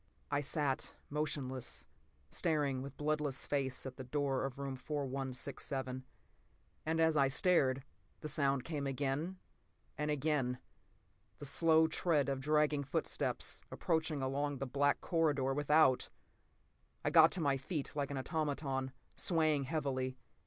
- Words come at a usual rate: No, slow, 130 wpm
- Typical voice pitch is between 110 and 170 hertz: Yes, medium, 140 Hz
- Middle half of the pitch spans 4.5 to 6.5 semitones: No, narrow, 2.4 semitones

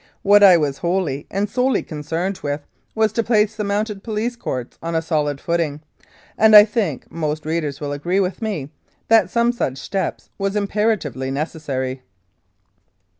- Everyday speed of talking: Yes, average, 160 wpm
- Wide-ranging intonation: Yes, wide, 6.1 semitones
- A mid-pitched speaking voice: Yes, medium, 175 Hz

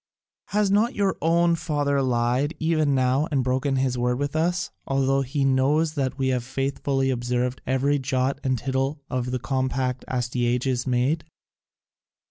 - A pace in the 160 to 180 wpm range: No, average, 150 wpm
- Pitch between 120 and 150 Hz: Yes, low, 135 Hz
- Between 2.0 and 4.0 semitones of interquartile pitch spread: Yes, narrow, 2.4 semitones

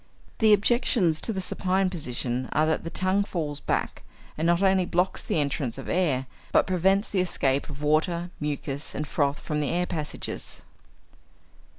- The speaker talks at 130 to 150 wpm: No, average, 170 wpm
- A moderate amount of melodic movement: Yes, average, 4.2 semitones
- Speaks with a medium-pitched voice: Yes, medium, 165 Hz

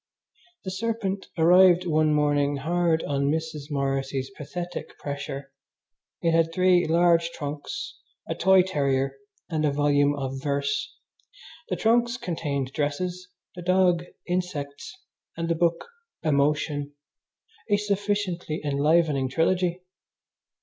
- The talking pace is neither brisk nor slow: No, slow, 115 wpm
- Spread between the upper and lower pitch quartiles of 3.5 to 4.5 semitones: Yes, average, 4.0 semitones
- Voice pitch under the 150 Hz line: No, medium, 160 Hz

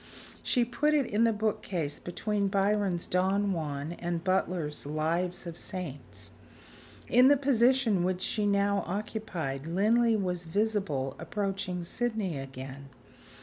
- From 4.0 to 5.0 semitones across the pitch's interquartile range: Yes, average, 4.3 semitones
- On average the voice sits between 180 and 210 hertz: Yes, high, 190 Hz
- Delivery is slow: Yes, slow, 130 wpm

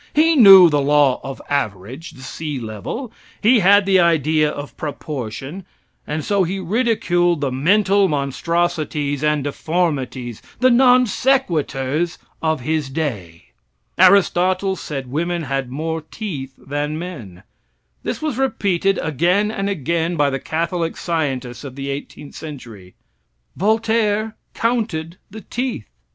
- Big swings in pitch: Yes, wide, 5.9 semitones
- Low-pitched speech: No, medium, 160 Hz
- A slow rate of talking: Yes, slow, 130 wpm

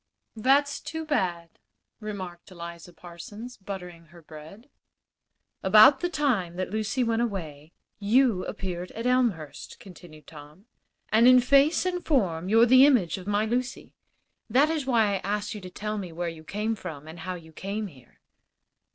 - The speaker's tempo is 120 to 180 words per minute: Yes, average, 160 wpm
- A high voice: Yes, high, 200 Hz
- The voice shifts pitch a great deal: Yes, wide, 5.8 semitones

